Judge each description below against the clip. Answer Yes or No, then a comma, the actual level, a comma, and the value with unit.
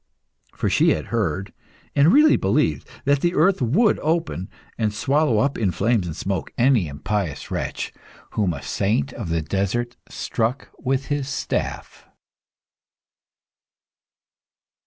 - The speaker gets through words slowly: Yes, slow, 130 wpm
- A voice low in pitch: Yes, low, 115 Hz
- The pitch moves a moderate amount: No, wide, 6.6 semitones